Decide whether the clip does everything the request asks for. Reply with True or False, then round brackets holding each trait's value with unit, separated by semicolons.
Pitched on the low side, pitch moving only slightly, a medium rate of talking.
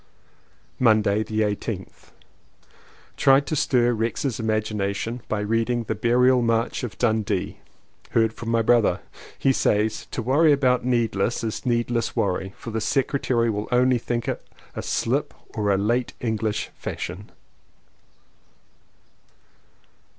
False (115 Hz; 2.3 semitones; 125 wpm)